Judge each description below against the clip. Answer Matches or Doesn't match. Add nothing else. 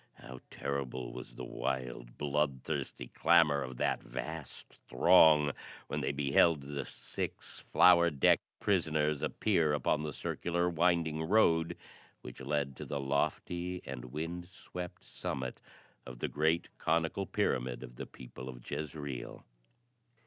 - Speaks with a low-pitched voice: Matches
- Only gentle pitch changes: Doesn't match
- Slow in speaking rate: Matches